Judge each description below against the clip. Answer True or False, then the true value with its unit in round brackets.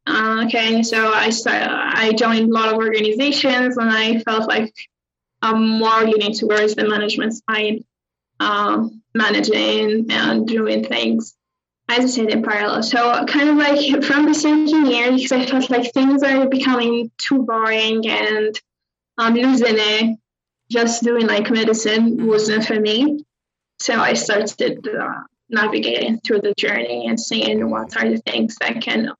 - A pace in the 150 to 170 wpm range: True (155 wpm)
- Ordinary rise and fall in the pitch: False (2.1 semitones)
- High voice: True (225 Hz)